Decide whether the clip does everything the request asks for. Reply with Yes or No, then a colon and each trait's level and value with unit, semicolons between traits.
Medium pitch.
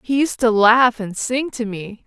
No: high, 235 Hz